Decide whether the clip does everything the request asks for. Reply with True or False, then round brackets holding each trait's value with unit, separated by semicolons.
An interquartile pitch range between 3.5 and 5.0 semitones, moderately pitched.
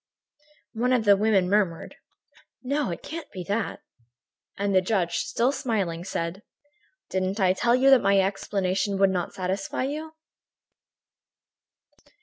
False (4.3 semitones; 200 Hz)